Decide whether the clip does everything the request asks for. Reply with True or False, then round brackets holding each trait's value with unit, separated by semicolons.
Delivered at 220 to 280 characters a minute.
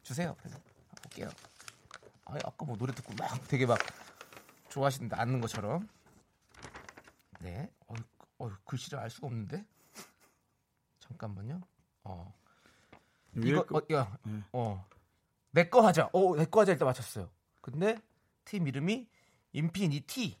True (225 characters per minute)